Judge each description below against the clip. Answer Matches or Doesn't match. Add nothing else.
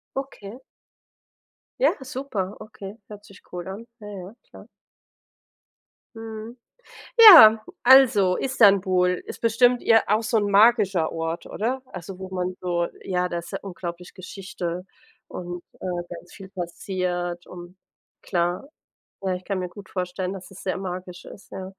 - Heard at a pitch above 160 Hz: Matches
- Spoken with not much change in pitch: Doesn't match